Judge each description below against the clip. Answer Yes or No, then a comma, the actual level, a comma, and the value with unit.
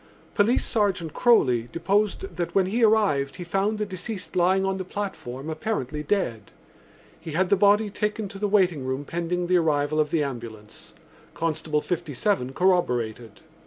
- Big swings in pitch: Yes, wide, 5.7 semitones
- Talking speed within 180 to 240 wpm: No, average, 160 wpm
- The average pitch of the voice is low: No, medium, 175 Hz